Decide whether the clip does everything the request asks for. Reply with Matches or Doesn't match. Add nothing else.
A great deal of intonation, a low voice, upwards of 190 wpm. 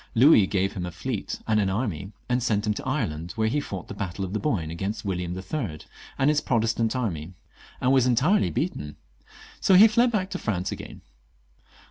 Matches